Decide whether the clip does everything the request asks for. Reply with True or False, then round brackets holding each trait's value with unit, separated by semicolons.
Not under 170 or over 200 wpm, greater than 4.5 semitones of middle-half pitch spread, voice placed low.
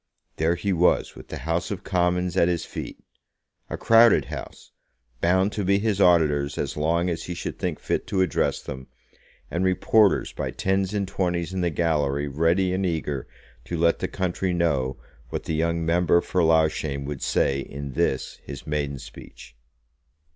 False (175 wpm; 3.7 semitones; 85 Hz)